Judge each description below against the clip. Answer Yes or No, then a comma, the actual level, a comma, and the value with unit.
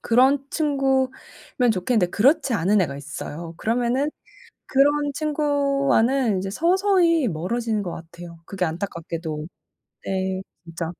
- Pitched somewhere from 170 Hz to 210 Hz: No, high, 230 Hz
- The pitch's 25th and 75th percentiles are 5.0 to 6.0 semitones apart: No, wide, 7.9 semitones